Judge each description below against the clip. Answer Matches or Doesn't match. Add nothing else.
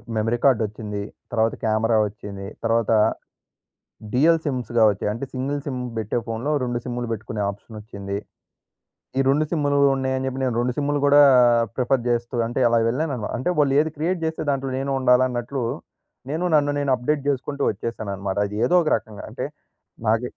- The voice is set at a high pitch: Doesn't match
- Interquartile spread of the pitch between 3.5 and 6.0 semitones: Matches